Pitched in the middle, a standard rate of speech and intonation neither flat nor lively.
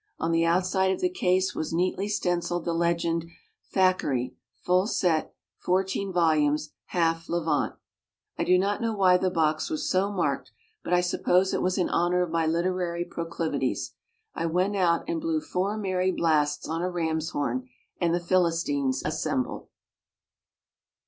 No: medium, 175 Hz; average, 155 wpm; narrow, 2.2 semitones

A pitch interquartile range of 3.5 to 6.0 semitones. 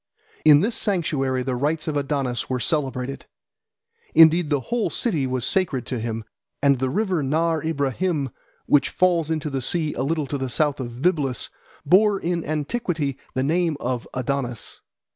Yes: average, 4.0 semitones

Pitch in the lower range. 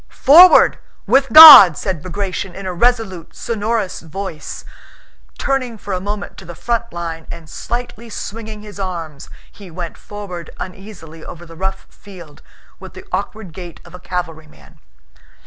No: high, 190 Hz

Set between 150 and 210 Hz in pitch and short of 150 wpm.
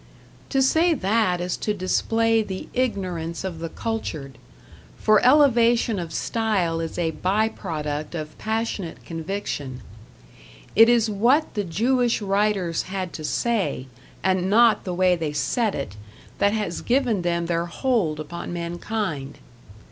Yes: high, 190 Hz; average, 140 wpm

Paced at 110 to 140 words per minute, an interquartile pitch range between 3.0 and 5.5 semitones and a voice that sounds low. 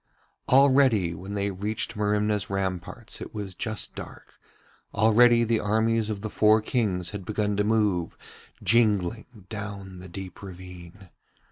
No: slow, 135 wpm; narrow, 2.6 semitones; low, 105 Hz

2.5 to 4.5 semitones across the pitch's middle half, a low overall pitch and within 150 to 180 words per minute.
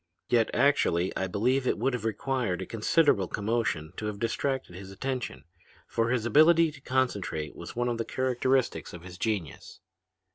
No: average, 5.1 semitones; low, 115 Hz; average, 170 wpm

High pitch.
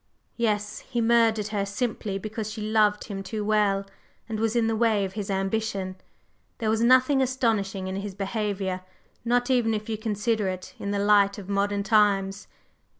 Yes: high, 210 Hz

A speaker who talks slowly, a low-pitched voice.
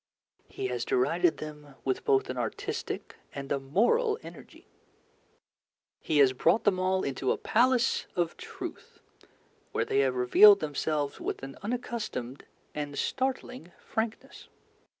No: slow, 130 wpm; medium, 160 Hz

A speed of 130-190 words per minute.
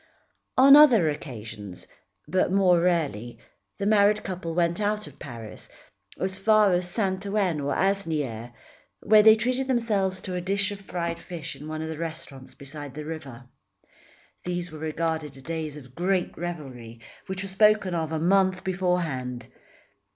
Yes: average, 160 wpm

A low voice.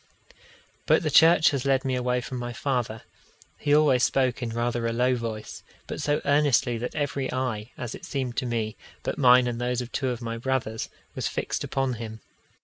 Yes: low, 125 Hz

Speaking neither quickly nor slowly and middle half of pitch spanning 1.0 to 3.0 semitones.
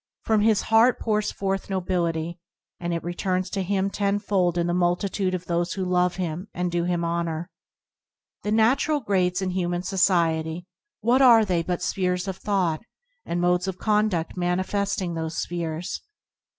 Yes: average, 165 wpm; narrow, 2.5 semitones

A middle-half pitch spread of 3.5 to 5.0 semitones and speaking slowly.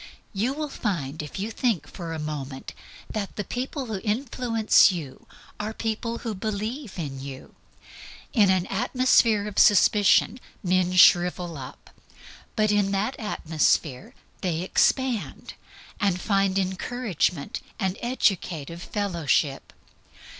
Yes: average, 4.7 semitones; slow, 120 wpm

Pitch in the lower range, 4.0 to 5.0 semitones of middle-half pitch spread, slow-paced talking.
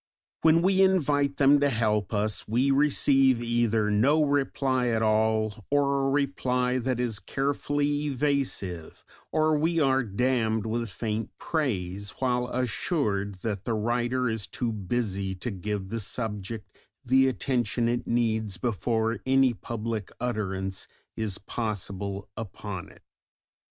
Yes: low, 120 Hz; average, 4.3 semitones; slow, 130 wpm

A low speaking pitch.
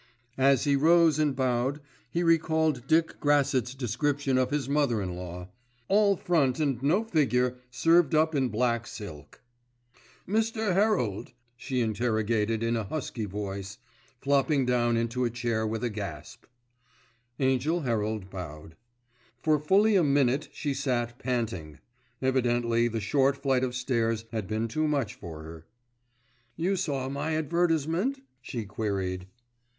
Yes: low, 130 Hz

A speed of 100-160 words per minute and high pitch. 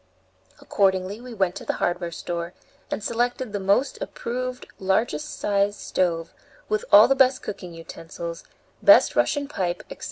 Yes: average, 150 wpm; high, 200 Hz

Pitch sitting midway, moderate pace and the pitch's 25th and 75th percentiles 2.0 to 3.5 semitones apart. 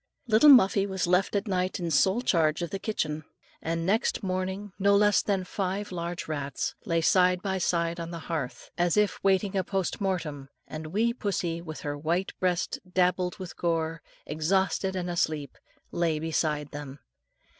Yes: medium, 180 Hz; average, 170 wpm; average, 2.9 semitones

